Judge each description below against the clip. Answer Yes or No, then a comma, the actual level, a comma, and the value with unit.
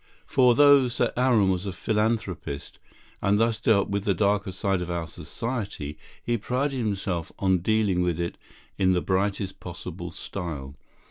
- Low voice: Yes, low, 100 Hz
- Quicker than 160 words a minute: No, average, 155 wpm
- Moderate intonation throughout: Yes, average, 4.1 semitones